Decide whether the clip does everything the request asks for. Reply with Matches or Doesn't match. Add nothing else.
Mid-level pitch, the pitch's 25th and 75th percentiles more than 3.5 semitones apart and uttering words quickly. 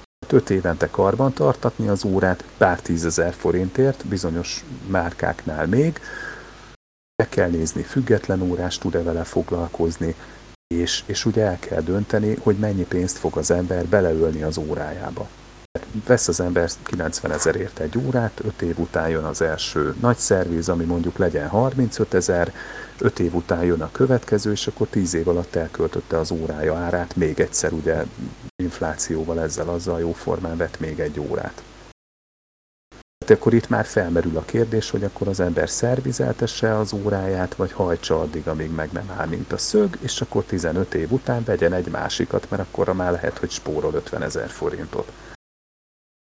Doesn't match